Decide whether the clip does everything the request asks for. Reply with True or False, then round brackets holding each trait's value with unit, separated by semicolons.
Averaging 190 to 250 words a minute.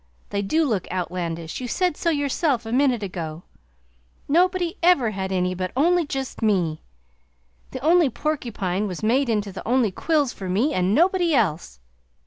False (160 wpm)